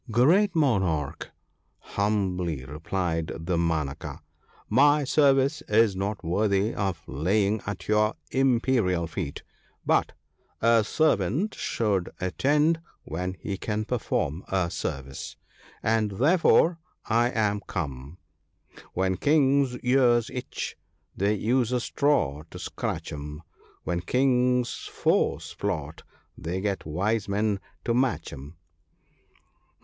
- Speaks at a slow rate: Yes, slow, 120 wpm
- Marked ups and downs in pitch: Yes, wide, 6.3 semitones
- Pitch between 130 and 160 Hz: No, low, 105 Hz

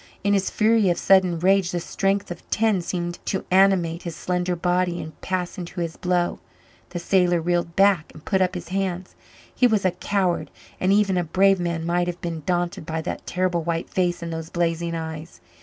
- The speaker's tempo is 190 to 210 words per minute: Yes, average, 200 wpm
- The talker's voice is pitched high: No, medium, 175 Hz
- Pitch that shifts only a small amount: Yes, narrow, 1.9 semitones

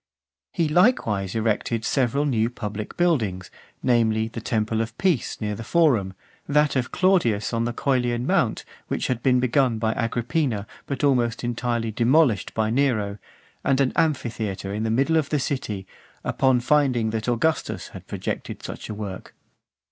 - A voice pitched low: Yes, low, 120 Hz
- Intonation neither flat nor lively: Yes, average, 4.0 semitones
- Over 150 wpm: Yes, average, 165 wpm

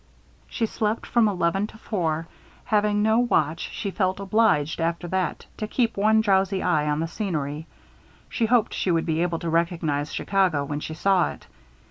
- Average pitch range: Yes, average, 4.5 semitones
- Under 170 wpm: No, average, 175 wpm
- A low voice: No, medium, 185 Hz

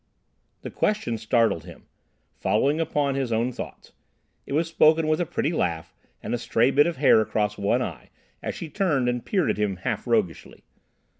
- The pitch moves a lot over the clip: Yes, wide, 6.2 semitones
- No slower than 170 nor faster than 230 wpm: Yes, average, 180 wpm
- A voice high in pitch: No, low, 125 Hz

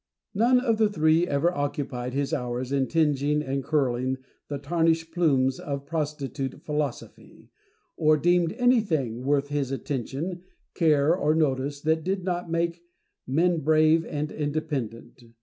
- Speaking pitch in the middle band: Yes, medium, 150 Hz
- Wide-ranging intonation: No, average, 3.2 semitones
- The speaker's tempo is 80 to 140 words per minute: Yes, slow, 135 wpm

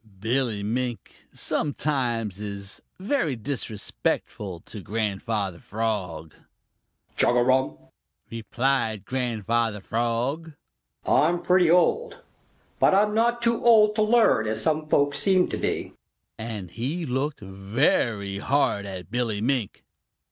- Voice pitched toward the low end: Yes, low, 120 Hz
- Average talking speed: No, slow, 110 wpm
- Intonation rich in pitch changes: Yes, wide, 6.6 semitones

